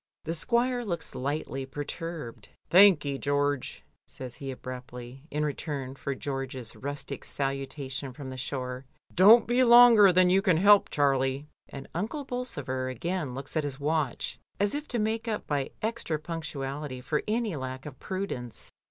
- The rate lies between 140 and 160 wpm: Yes, average, 155 wpm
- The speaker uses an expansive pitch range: Yes, wide, 6.2 semitones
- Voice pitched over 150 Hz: No, medium, 145 Hz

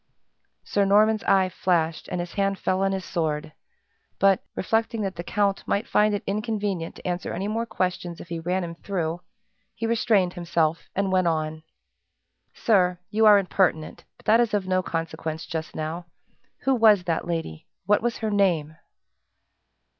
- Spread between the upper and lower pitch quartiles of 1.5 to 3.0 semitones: No, average, 3.6 semitones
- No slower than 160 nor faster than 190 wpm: Yes, average, 170 wpm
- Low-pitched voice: No, medium, 185 Hz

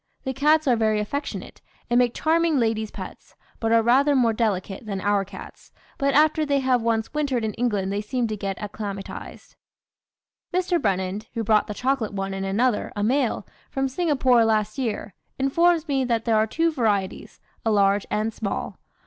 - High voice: Yes, high, 230 Hz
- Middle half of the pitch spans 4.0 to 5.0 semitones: Yes, average, 4.5 semitones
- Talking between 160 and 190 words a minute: Yes, average, 180 wpm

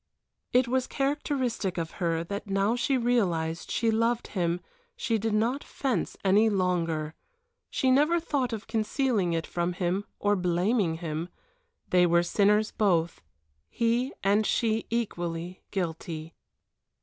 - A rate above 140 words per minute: No, slow, 135 wpm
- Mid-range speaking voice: No, high, 205 Hz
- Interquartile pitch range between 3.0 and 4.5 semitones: No, average, 5.3 semitones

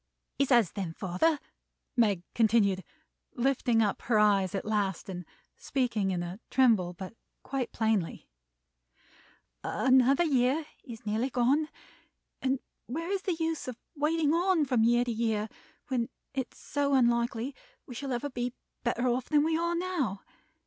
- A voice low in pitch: No, high, 245 Hz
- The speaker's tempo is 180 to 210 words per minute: No, average, 150 wpm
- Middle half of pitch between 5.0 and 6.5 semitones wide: No, average, 4.6 semitones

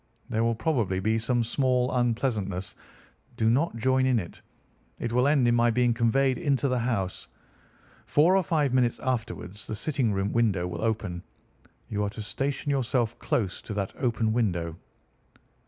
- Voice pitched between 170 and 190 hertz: No, low, 115 Hz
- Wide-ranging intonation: No, average, 3.7 semitones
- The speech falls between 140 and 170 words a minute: Yes, average, 165 wpm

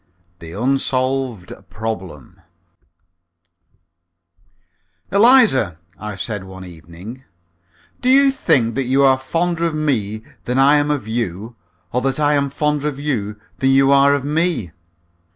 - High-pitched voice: No, low, 130 Hz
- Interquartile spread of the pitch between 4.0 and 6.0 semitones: Yes, wide, 5.5 semitones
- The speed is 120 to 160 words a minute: Yes, slow, 135 wpm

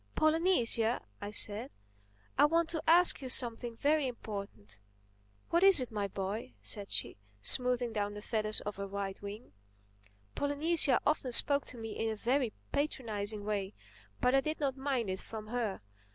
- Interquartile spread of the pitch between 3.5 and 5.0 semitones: No, wide, 5.5 semitones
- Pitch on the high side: Yes, high, 230 Hz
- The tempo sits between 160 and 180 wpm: Yes, average, 165 wpm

